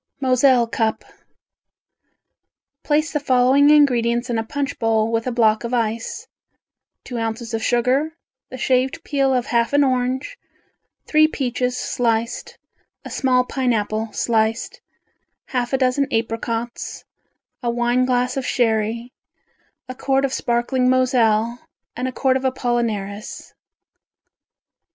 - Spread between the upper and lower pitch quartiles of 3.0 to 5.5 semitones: No, narrow, 2.4 semitones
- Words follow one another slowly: Yes, slow, 125 wpm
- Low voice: No, high, 245 Hz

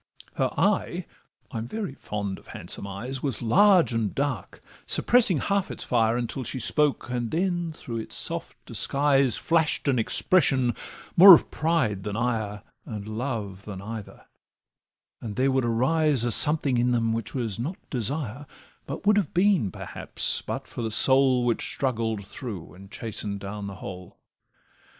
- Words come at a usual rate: Yes, average, 155 wpm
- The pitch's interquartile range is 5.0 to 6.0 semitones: Yes, average, 5.3 semitones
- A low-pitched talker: Yes, low, 120 Hz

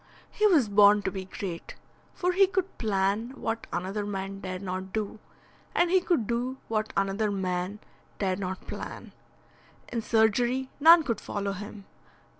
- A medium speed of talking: Yes, average, 155 wpm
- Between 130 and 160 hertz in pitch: No, high, 210 Hz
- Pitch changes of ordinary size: Yes, average, 4.1 semitones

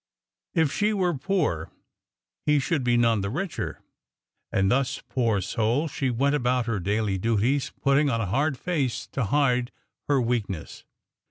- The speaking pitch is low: Yes, low, 125 Hz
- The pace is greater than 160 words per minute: No, average, 155 wpm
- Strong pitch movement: No, average, 4.5 semitones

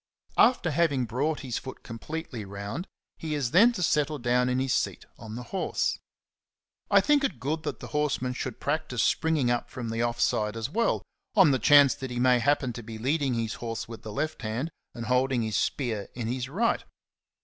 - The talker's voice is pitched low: Yes, low, 130 Hz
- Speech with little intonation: No, average, 4.5 semitones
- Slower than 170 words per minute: No, fast, 205 wpm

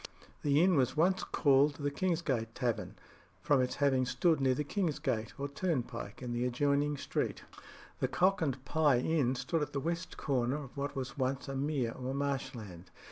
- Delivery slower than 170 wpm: No, average, 185 wpm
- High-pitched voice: No, medium, 140 Hz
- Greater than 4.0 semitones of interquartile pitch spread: No, average, 2.8 semitones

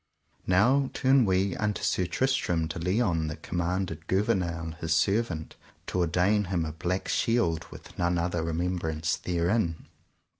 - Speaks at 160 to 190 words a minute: No, average, 140 wpm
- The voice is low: Yes, very low, 90 Hz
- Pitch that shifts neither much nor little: Yes, average, 3.4 semitones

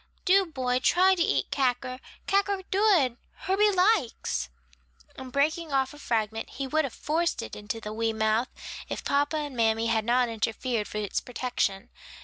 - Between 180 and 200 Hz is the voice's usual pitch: No, very high, 255 Hz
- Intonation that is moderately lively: No, wide, 6.6 semitones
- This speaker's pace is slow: No, average, 165 wpm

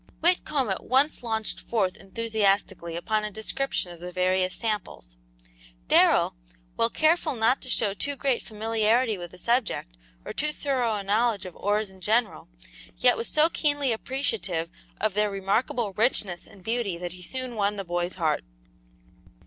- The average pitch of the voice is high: Yes, high, 215 Hz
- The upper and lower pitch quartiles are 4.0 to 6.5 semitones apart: Yes, average, 4.6 semitones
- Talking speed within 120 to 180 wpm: Yes, average, 160 wpm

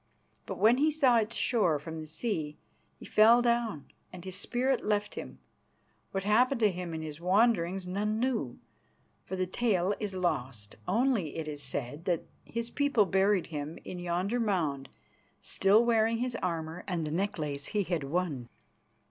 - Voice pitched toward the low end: No, high, 190 Hz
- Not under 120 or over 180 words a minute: Yes, average, 165 wpm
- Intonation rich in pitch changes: Yes, wide, 6.0 semitones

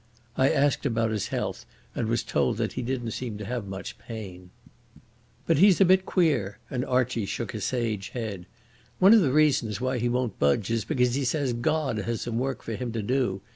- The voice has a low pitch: Yes, low, 120 Hz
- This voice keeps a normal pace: No, fast, 210 wpm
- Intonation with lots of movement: No, average, 3.6 semitones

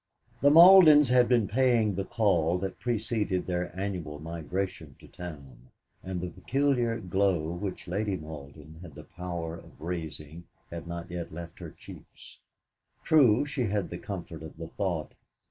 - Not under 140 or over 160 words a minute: Yes, average, 155 wpm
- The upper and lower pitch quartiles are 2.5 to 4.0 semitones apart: No, average, 4.8 semitones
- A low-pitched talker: Yes, very low, 90 Hz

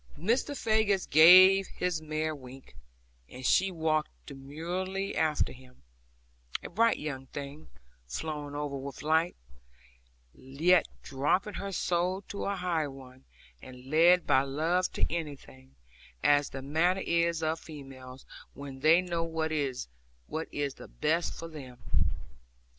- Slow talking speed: Yes, slow, 130 wpm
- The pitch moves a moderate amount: Yes, average, 4.3 semitones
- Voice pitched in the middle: Yes, medium, 155 Hz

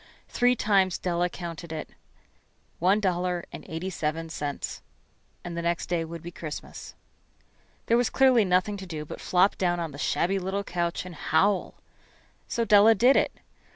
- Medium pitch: Yes, medium, 180 Hz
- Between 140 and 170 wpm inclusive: Yes, average, 165 wpm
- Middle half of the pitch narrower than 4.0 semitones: Yes, average, 3.0 semitones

